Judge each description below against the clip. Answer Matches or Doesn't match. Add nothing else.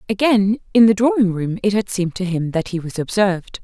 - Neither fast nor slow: Doesn't match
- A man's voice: Doesn't match